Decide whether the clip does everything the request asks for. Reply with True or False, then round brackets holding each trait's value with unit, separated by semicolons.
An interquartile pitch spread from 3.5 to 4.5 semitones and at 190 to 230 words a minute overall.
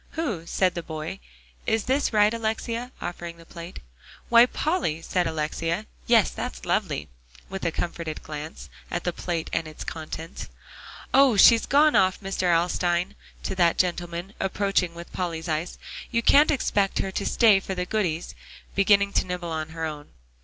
False (3.8 semitones; 165 wpm)